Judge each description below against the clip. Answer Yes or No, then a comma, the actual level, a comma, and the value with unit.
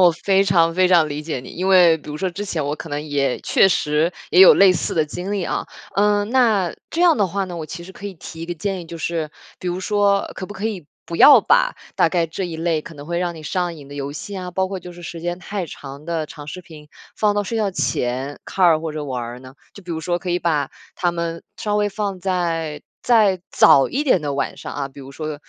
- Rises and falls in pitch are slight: No, average, 3.9 semitones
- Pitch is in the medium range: Yes, medium, 175 Hz